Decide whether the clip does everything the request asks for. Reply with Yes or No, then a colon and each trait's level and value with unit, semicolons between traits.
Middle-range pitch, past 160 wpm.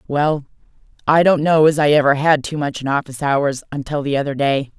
Yes: medium, 145 Hz; average, 200 wpm